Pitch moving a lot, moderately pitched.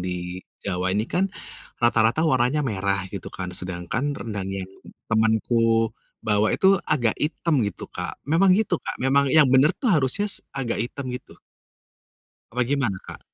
No: wide, 6.1 semitones; low, 120 Hz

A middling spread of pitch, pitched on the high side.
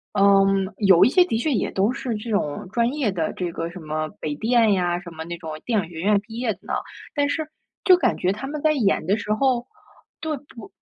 No: wide, 5.8 semitones; high, 210 Hz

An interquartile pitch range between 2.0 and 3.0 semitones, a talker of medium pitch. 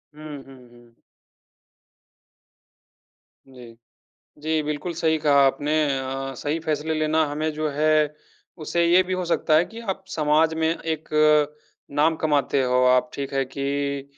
Yes: narrow, 2.5 semitones; medium, 150 Hz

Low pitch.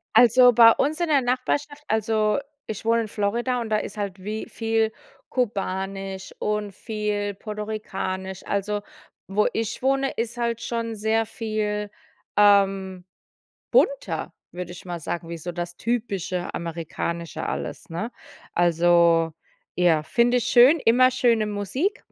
No: high, 210 Hz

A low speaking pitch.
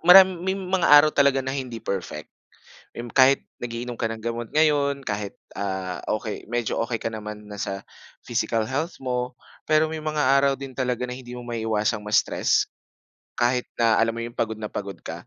Yes: low, 120 Hz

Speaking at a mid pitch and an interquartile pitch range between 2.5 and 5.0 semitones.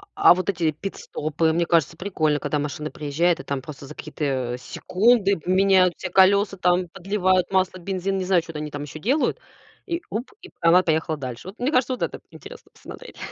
Yes: medium, 180 Hz; average, 4.1 semitones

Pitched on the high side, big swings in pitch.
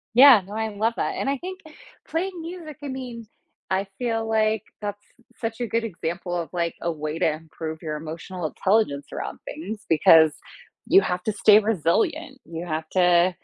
Yes: high, 205 Hz; wide, 5.8 semitones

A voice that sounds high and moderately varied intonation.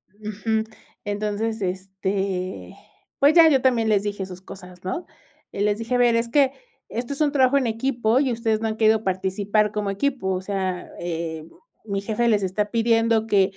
Yes: high, 215 Hz; average, 3.3 semitones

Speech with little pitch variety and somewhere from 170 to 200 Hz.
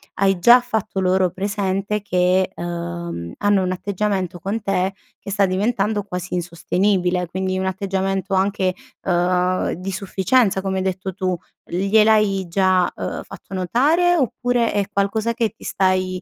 Yes: narrow, 2.0 semitones; high, 190 Hz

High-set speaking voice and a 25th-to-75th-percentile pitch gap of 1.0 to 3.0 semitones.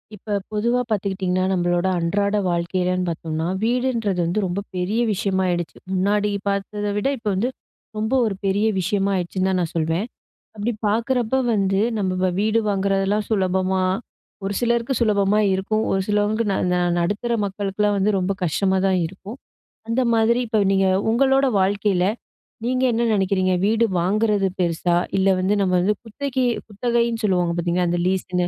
Yes: high, 200 Hz; average, 2.7 semitones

